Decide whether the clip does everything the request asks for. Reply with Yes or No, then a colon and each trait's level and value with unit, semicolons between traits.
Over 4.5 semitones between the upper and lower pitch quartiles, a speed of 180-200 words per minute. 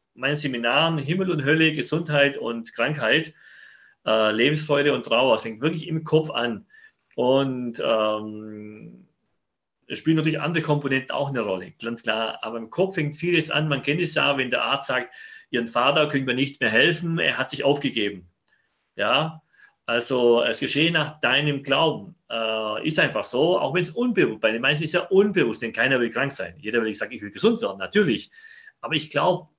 Yes: wide, 5.6 semitones; fast, 190 wpm